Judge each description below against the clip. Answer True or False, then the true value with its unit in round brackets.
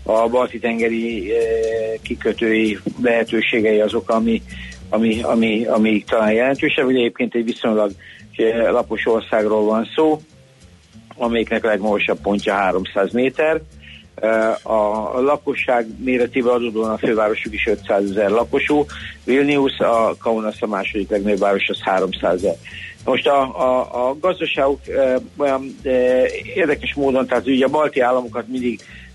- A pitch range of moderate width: True (3.0 semitones)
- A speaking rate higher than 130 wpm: False (125 wpm)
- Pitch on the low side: True (115 Hz)